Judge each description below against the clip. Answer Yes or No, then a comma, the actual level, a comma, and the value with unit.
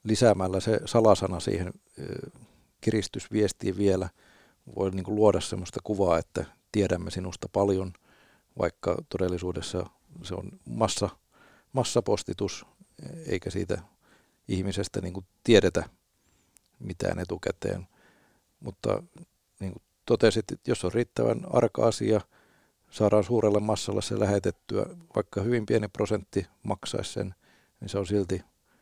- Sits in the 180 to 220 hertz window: No, low, 100 Hz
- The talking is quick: No, average, 115 wpm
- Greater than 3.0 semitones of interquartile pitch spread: No, average, 2.7 semitones